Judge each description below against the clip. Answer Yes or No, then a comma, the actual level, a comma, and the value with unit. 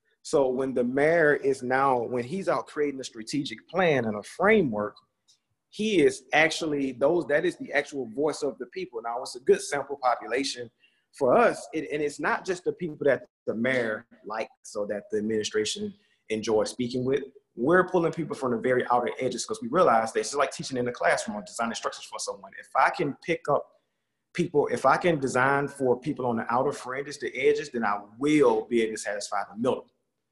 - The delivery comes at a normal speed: No, fast, 210 wpm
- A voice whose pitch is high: No, medium, 140 Hz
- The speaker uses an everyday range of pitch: No, wide, 6.1 semitones